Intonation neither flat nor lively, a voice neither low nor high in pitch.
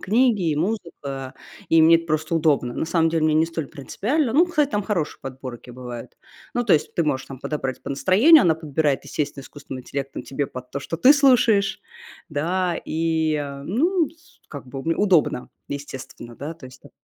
No: wide, 6.1 semitones; medium, 160 Hz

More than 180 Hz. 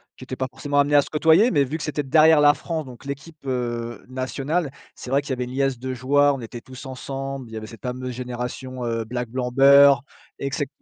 No: low, 135 Hz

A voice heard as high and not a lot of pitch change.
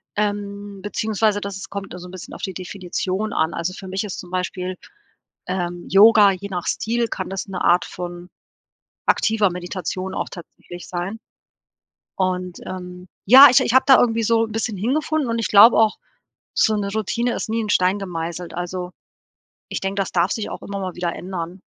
No: high, 195 Hz; average, 3.1 semitones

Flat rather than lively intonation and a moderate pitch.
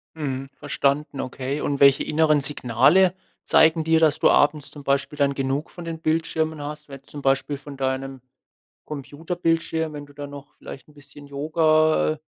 Yes: narrow, 2.2 semitones; medium, 145 Hz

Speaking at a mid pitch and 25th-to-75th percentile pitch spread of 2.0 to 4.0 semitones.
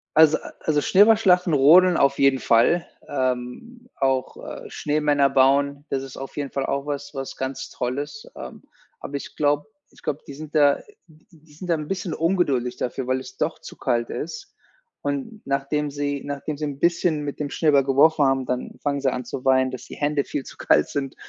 Yes: medium, 145 Hz; narrow, 2.4 semitones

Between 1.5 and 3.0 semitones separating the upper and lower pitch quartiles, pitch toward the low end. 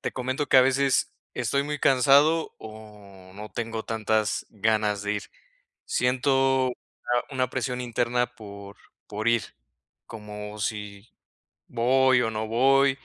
No: average, 3.8 semitones; low, 115 Hz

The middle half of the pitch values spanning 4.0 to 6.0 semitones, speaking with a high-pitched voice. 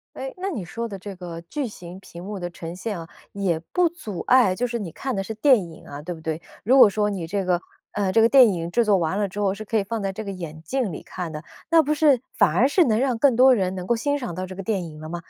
Yes: average, 5.2 semitones; high, 200 Hz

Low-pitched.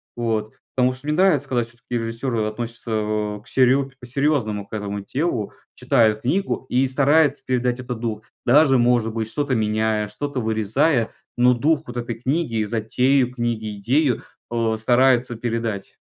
Yes: low, 120 Hz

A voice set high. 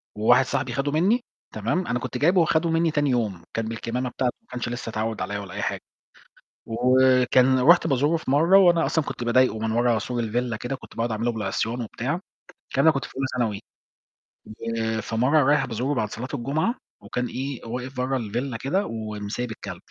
No: low, 125 Hz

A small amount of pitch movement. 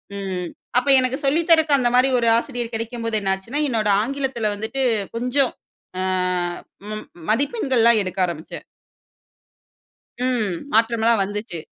No: average, 3.5 semitones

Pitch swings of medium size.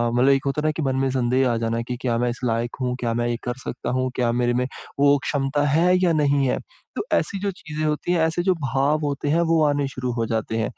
Yes: average, 3.6 semitones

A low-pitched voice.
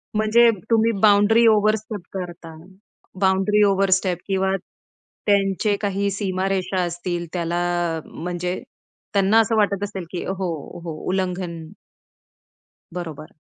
No: high, 190 Hz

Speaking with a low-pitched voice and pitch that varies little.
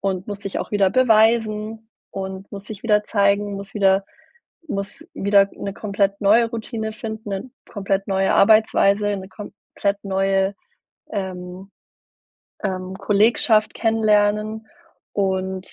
No: high, 200 Hz; narrow, 1.8 semitones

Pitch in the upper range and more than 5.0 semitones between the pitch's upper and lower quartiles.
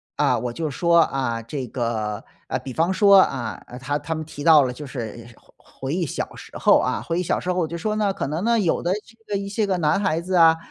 No: medium, 160 Hz; wide, 5.5 semitones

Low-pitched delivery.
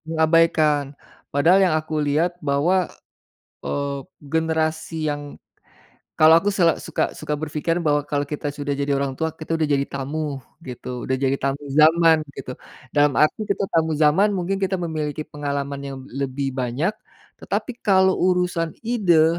No: medium, 155 Hz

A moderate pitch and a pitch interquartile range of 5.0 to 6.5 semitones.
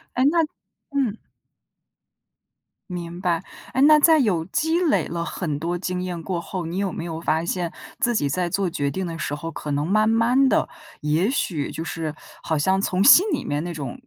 Yes: medium, 180 Hz; wide, 5.6 semitones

